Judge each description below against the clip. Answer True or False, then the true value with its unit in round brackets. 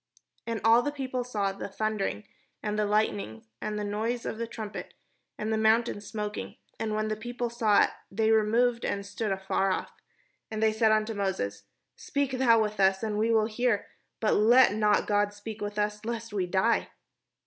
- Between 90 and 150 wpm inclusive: False (195 wpm)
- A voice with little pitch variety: True (1.9 semitones)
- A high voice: True (215 Hz)